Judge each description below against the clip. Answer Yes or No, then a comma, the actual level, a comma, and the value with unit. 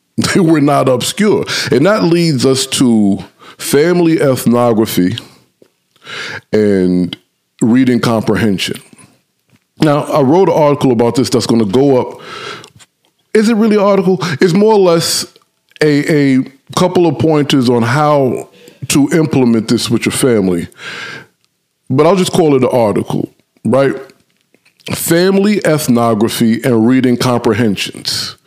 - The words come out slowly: Yes, slow, 130 wpm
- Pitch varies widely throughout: Yes, wide, 6.3 semitones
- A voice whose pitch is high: No, low, 135 Hz